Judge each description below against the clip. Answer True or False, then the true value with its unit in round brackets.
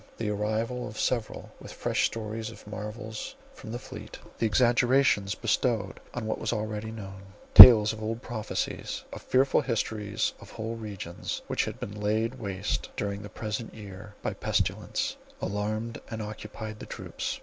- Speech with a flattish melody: True (1.6 semitones)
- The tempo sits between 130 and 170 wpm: True (160 wpm)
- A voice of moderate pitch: False (110 Hz)